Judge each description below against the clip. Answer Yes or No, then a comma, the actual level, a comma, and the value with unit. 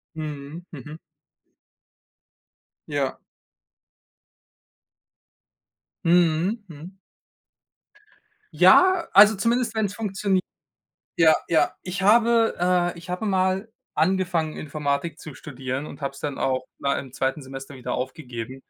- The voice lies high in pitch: No, medium, 160 Hz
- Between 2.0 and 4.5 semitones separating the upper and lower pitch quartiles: No, wide, 5.6 semitones